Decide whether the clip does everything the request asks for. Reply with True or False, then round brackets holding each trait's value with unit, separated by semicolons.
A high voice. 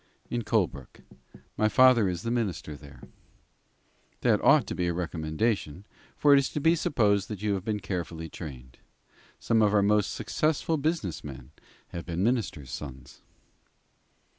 False (100 Hz)